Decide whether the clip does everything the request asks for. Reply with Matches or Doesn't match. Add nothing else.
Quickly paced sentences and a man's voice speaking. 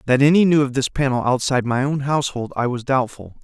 Matches